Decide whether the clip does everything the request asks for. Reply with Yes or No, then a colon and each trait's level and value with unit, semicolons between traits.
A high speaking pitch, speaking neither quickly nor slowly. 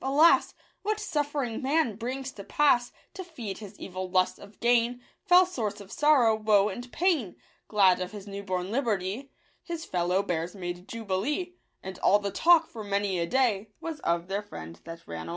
Yes: high, 215 Hz; average, 190 wpm